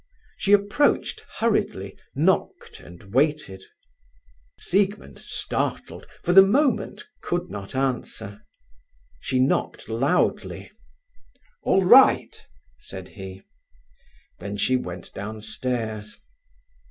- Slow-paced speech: Yes, slow, 90 wpm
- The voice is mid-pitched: No, low, 130 Hz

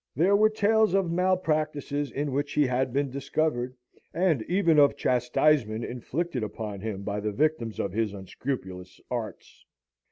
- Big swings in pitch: Yes, wide, 6.1 semitones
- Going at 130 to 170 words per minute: Yes, average, 150 wpm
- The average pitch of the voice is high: No, medium, 140 Hz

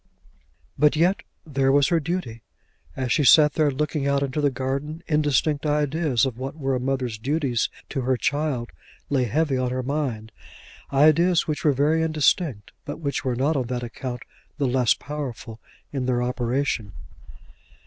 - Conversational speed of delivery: Yes, average, 165 wpm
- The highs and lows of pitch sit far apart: No, average, 3.1 semitones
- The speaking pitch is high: No, medium, 140 Hz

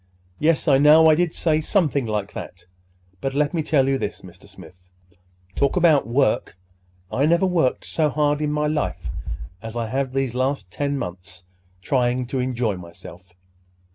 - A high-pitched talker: No, low, 135 Hz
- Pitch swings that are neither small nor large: No, wide, 6.8 semitones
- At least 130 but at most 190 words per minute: Yes, average, 165 wpm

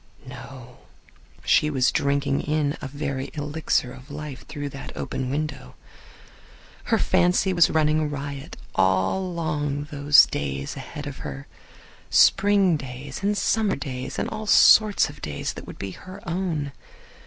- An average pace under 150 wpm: Yes, average, 140 wpm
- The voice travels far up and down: No, average, 3.1 semitones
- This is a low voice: No, medium, 145 Hz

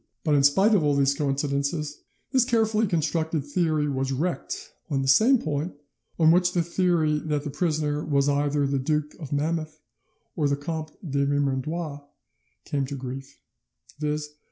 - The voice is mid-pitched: Yes, medium, 150 Hz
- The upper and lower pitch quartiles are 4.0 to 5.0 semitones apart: No, average, 2.7 semitones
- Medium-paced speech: Yes, average, 160 wpm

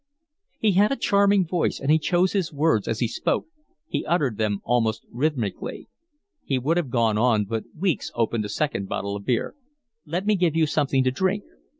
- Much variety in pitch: Yes, wide, 7.6 semitones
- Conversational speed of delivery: Yes, average, 195 wpm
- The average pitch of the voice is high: No, medium, 140 Hz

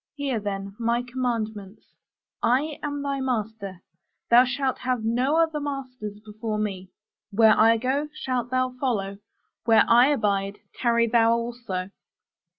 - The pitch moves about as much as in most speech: Yes, average, 3.4 semitones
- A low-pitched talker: No, high, 235 Hz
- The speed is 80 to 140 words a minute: Yes, slow, 135 wpm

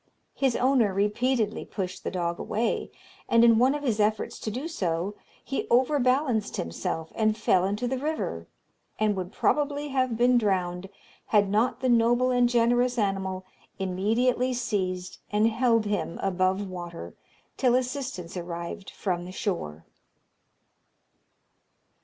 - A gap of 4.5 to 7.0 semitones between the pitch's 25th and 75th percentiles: Yes, average, 4.9 semitones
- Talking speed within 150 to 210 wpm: No, slow, 135 wpm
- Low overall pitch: No, high, 215 Hz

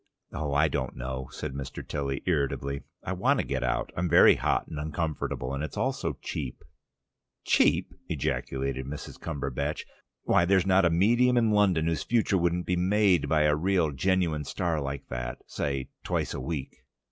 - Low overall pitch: Yes, very low, 80 Hz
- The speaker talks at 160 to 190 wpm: Yes, average, 175 wpm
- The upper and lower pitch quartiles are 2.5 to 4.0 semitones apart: No, average, 4.8 semitones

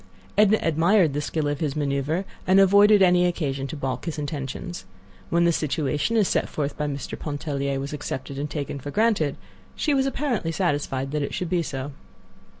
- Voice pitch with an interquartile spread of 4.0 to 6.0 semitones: Yes, average, 4.3 semitones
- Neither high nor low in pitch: Yes, medium, 150 Hz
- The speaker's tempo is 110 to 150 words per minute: No, average, 185 wpm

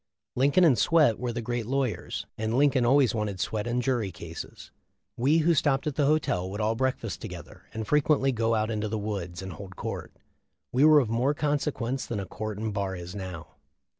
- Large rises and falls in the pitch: No, average, 4.8 semitones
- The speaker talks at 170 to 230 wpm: Yes, average, 200 wpm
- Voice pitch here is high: No, low, 115 Hz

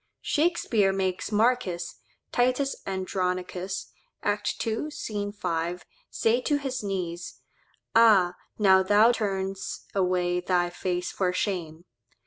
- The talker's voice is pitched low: No, high, 190 Hz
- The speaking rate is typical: No, slow, 110 wpm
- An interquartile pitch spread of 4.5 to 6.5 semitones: No, average, 3.7 semitones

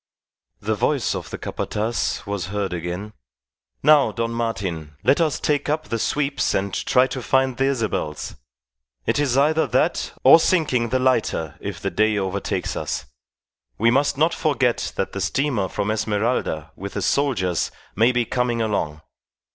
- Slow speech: No, average, 160 wpm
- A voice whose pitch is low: Yes, low, 115 Hz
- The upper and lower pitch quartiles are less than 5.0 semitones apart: No, wide, 5.4 semitones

